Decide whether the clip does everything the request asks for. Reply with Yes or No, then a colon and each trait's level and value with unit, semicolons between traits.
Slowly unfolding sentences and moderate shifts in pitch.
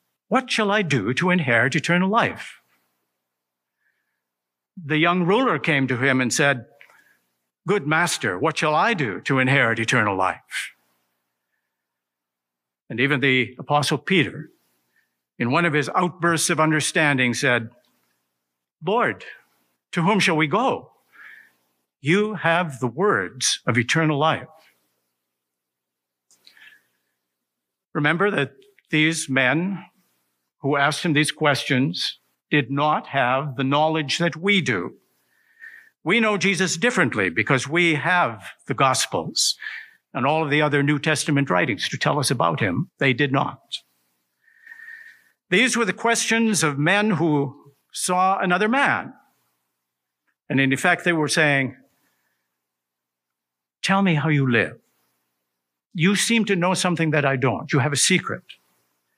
No: slow, 130 wpm; wide, 7.5 semitones